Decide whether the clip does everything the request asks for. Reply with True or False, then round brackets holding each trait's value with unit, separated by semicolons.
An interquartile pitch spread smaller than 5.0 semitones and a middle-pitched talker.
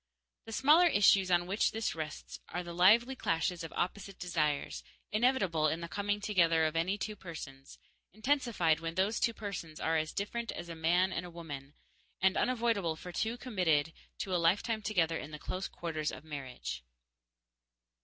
True (4.3 semitones; 180 Hz)